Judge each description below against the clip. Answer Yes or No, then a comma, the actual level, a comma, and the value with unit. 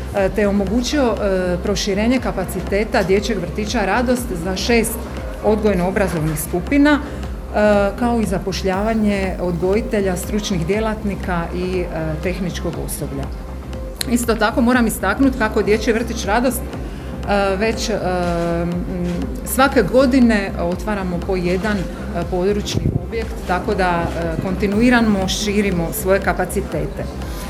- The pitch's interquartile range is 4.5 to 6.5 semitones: No, average, 3.2 semitones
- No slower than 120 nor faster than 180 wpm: No, slow, 110 wpm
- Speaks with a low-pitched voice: No, high, 195 Hz